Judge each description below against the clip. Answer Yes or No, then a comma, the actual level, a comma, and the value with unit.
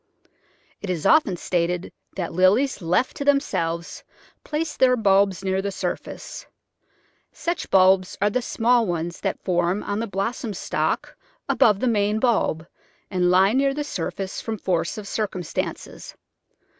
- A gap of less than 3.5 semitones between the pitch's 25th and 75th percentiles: No, average, 4.5 semitones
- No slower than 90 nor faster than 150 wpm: Yes, average, 145 wpm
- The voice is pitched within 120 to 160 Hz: No, high, 195 Hz